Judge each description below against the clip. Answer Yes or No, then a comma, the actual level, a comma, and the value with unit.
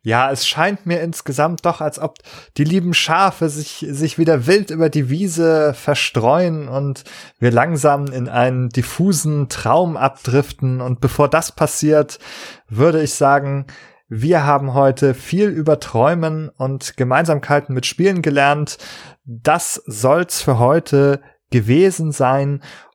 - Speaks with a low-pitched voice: No, medium, 145 Hz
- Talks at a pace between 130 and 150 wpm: Yes, average, 135 wpm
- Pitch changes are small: No, average, 3.2 semitones